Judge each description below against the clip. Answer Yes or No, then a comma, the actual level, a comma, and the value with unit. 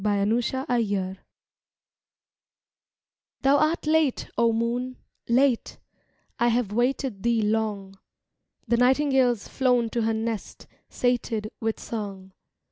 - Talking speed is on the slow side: Yes, slow, 110 wpm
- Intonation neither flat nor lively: Yes, average, 3.1 semitones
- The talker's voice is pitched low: No, high, 235 Hz